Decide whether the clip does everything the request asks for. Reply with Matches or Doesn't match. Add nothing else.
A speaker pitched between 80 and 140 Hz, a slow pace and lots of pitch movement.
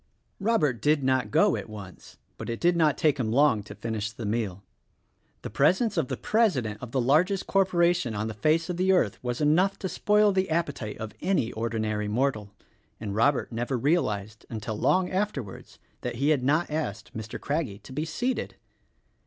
Doesn't match